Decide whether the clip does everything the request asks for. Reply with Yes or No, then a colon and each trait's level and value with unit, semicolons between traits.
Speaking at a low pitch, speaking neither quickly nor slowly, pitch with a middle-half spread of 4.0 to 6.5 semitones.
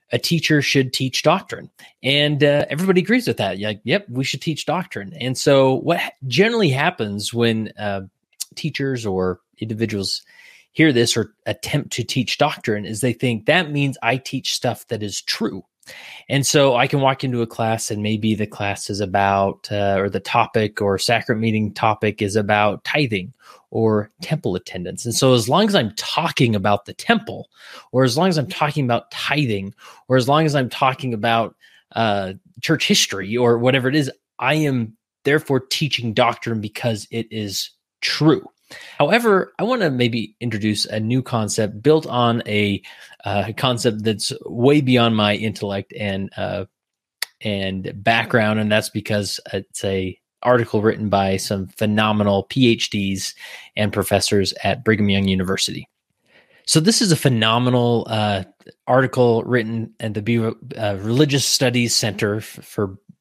Yes: low, 115 Hz; average, 165 wpm; average, 4.3 semitones